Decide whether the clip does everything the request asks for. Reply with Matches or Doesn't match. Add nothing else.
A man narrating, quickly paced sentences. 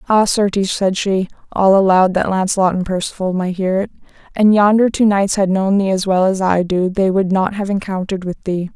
Doesn't match